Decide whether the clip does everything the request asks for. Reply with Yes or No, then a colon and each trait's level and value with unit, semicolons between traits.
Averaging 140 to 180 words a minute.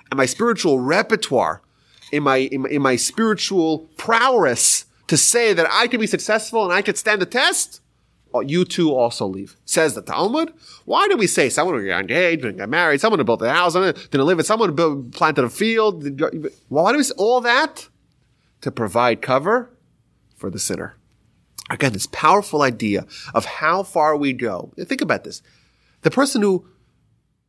No: average, 190 wpm